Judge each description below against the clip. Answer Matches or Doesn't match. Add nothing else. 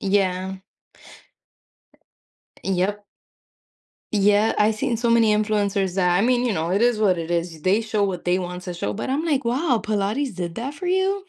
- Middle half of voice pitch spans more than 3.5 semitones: Matches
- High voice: Matches